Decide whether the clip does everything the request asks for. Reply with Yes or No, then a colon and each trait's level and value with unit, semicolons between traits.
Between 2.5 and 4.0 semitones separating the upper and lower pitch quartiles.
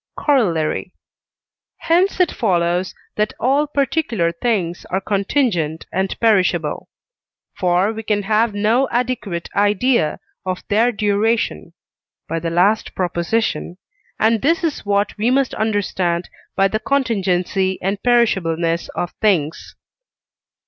No: average, 4.9 semitones